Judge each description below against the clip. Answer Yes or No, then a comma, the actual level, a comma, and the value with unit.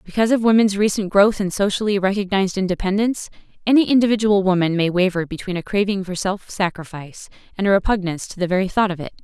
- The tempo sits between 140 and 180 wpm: No, average, 190 wpm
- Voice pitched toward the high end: Yes, high, 195 Hz